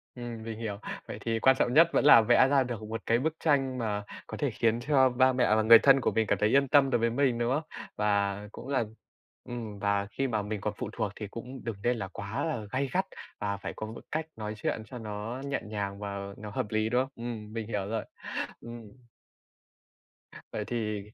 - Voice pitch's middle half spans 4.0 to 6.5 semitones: No, average, 3.4 semitones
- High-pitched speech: No, low, 115 Hz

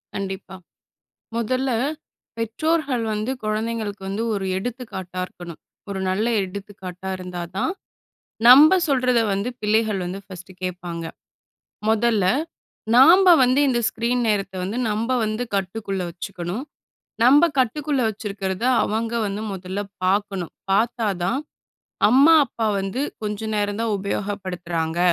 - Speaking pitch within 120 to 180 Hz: No, high, 210 Hz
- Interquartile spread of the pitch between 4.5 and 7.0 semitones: No, average, 3.8 semitones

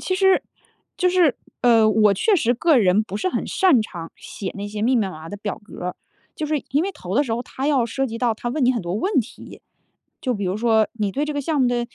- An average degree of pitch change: No, wide, 5.7 semitones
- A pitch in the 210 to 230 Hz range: No, high, 240 Hz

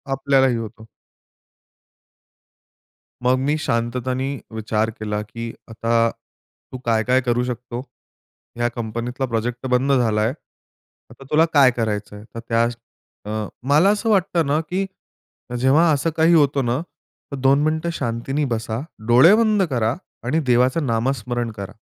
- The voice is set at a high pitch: No, low, 125 Hz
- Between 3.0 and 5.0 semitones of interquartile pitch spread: Yes, average, 3.5 semitones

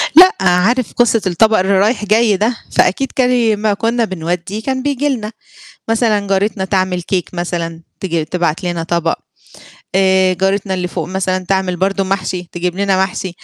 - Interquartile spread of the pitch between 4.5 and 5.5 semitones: No, average, 3.3 semitones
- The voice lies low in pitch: No, high, 190 Hz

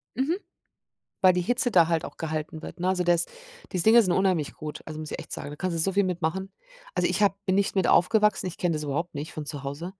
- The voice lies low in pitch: No, medium, 175 Hz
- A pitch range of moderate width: Yes, average, 3.5 semitones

